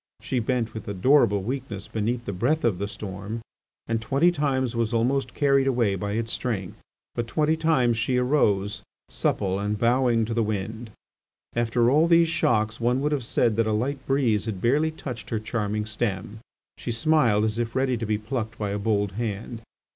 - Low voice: Yes, low, 115 Hz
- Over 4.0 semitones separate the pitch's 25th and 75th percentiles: No, average, 3.6 semitones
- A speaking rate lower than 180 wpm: No, average, 185 wpm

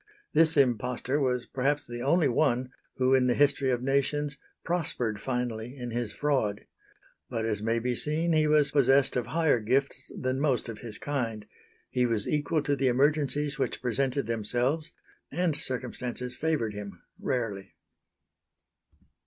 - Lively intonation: No, average, 3.4 semitones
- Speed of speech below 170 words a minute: Yes, average, 150 wpm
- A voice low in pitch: Yes, low, 130 Hz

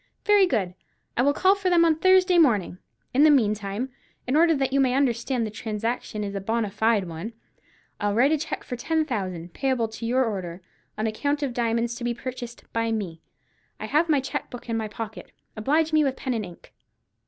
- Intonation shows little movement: No, average, 5.0 semitones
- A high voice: Yes, high, 240 Hz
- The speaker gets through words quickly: Yes, fast, 210 wpm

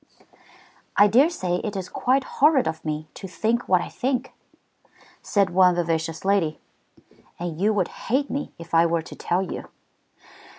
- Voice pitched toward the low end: No, high, 190 Hz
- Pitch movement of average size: No, wide, 6.0 semitones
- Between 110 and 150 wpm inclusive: No, average, 165 wpm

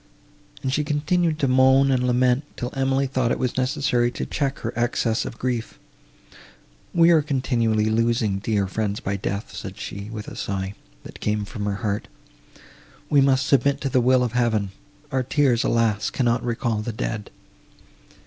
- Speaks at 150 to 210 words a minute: Yes, average, 165 wpm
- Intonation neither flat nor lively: Yes, average, 3.5 semitones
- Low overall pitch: Yes, low, 120 Hz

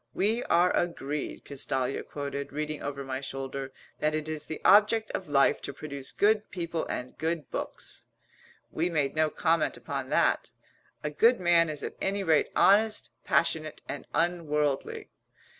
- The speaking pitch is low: No, medium, 155 Hz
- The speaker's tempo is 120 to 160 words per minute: Yes, average, 155 wpm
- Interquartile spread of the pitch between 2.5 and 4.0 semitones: Yes, average, 3.6 semitones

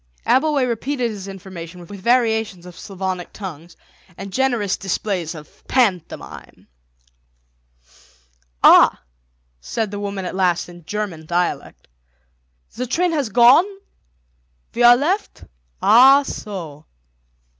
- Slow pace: Yes, slow, 110 wpm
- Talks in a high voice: Yes, high, 200 Hz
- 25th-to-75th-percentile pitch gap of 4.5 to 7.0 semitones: Yes, wide, 5.4 semitones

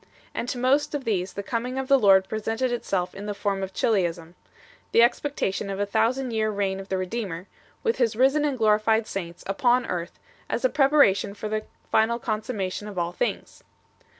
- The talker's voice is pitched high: Yes, high, 215 Hz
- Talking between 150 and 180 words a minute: No, average, 195 wpm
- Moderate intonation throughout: Yes, average, 4.1 semitones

